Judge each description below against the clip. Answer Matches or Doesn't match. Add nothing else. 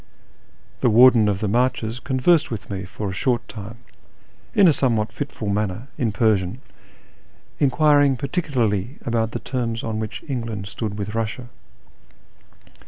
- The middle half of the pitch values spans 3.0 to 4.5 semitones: Matches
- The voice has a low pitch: Matches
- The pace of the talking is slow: Doesn't match